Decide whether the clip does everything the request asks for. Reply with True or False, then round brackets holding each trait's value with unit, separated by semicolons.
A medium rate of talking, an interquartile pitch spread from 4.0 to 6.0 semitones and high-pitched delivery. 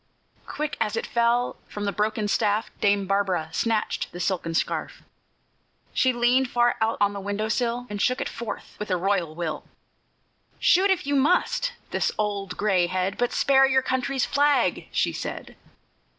True (165 wpm; 4.3 semitones; 215 Hz)